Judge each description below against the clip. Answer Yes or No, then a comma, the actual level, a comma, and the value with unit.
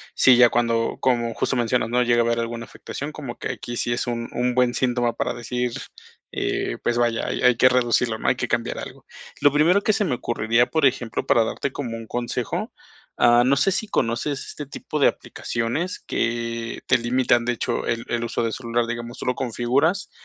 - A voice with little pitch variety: Yes, narrow, 1.7 semitones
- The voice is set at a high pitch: No, low, 120 Hz